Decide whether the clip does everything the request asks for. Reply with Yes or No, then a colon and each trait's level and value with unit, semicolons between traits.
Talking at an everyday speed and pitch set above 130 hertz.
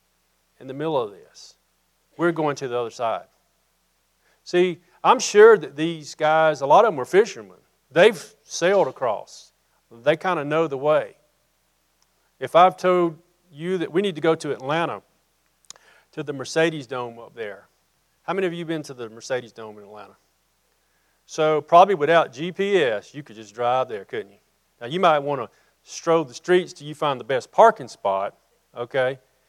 Yes: average, 175 wpm; medium, 140 Hz